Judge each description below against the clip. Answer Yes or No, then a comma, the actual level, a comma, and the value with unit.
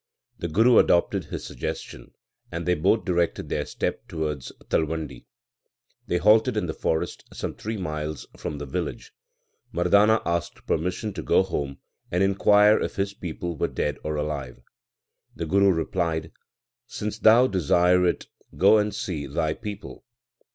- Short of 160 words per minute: Yes, average, 150 wpm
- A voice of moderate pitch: No, very low, 90 Hz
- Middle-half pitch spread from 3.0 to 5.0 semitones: Yes, average, 4.7 semitones